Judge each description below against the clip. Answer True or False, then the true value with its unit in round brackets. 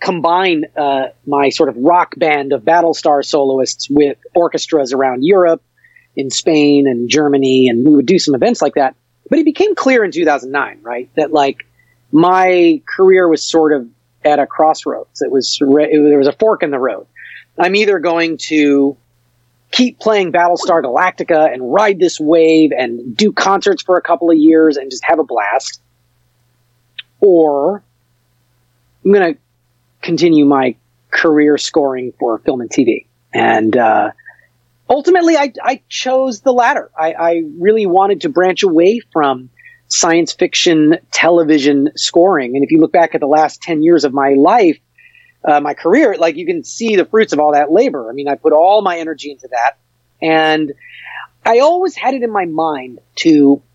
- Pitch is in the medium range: True (155 Hz)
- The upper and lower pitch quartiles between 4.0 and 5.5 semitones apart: True (4.7 semitones)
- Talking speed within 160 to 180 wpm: True (175 wpm)